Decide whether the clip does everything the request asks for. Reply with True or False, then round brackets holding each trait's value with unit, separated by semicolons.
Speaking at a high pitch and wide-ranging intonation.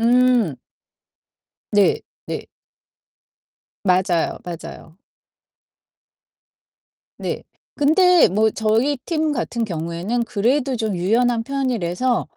True (225 Hz; 5.7 semitones)